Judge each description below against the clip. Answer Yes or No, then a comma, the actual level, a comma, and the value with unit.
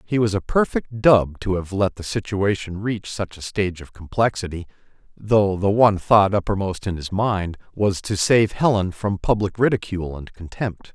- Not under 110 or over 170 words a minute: No, average, 180 wpm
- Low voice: Yes, low, 100 Hz